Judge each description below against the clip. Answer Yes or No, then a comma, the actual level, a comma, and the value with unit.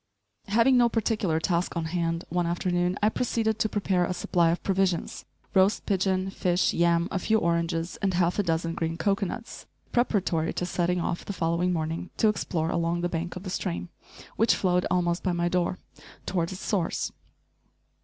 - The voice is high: No, medium, 180 Hz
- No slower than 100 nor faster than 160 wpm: No, average, 175 wpm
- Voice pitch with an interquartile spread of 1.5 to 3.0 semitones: Yes, narrow, 2.4 semitones